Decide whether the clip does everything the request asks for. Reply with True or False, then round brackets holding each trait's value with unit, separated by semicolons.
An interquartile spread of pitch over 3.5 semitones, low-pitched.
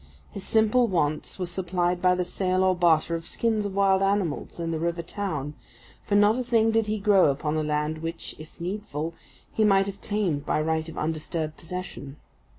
False (4.2 semitones; 180 Hz)